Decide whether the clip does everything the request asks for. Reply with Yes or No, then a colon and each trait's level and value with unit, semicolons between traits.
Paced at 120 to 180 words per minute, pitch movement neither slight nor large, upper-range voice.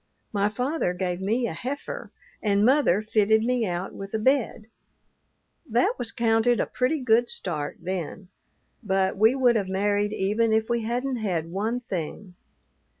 Yes: average, 155 wpm; average, 3.8 semitones; high, 220 Hz